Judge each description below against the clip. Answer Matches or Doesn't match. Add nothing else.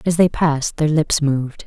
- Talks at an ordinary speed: Doesn't match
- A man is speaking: Doesn't match